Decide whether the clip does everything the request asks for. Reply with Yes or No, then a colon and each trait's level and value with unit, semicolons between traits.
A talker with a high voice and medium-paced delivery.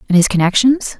Yes: high, 215 Hz; average, 180 wpm